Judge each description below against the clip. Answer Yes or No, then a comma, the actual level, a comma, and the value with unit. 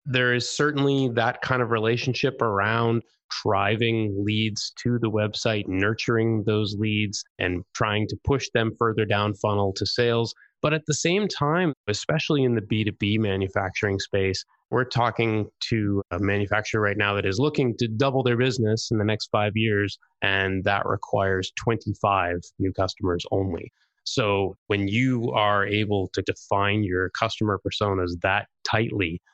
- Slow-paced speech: No, average, 155 wpm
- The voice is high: No, low, 105 Hz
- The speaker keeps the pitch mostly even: No, average, 3.0 semitones